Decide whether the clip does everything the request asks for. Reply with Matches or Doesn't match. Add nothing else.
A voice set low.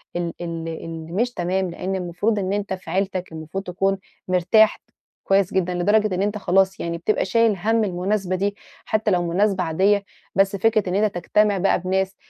Doesn't match